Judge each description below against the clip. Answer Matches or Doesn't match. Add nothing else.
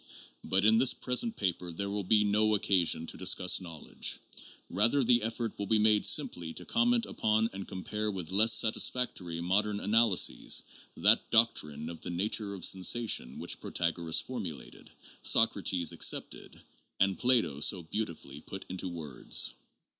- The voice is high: Doesn't match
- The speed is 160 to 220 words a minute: Doesn't match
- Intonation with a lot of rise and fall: Doesn't match